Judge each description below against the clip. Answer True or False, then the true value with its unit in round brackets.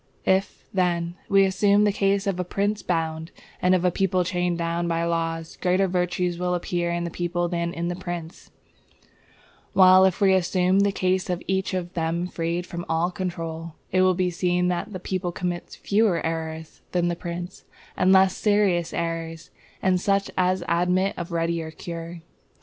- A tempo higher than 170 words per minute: True (180 wpm)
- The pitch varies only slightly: True (1.7 semitones)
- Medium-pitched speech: True (180 Hz)